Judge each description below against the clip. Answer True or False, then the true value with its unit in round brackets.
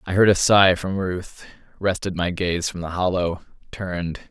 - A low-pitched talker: True (90 Hz)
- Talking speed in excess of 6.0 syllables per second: False (4.6 syllables/s)